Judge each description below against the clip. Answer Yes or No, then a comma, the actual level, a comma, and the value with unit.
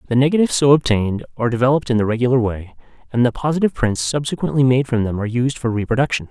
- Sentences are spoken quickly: Yes, fast, 210 wpm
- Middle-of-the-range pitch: No, low, 125 Hz